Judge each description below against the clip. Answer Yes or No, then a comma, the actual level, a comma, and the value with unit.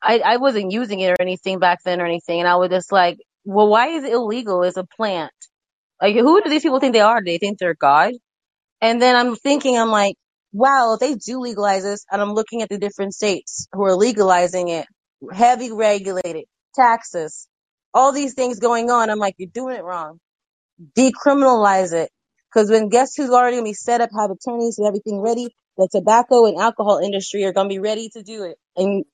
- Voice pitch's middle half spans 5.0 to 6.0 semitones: No, average, 4.0 semitones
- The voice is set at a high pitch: Yes, high, 210 Hz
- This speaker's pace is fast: Yes, fast, 215 wpm